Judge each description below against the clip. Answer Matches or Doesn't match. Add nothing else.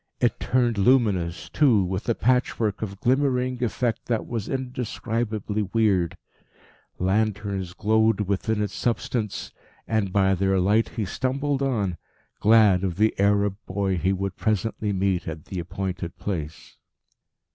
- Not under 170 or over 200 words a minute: Doesn't match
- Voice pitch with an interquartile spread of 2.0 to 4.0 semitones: Matches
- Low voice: Matches